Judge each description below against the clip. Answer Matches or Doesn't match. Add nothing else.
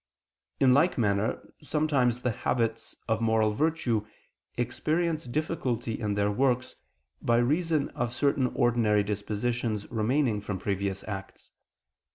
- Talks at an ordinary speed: Doesn't match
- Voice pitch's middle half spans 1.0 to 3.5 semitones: Doesn't match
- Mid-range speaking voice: Doesn't match